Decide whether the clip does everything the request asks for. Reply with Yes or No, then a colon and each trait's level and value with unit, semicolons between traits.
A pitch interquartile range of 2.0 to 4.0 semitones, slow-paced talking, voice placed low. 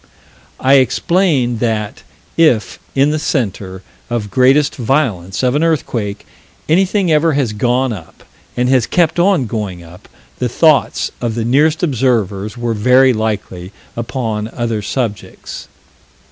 No: average, 5.2 semitones; slow, 130 wpm; low, 125 Hz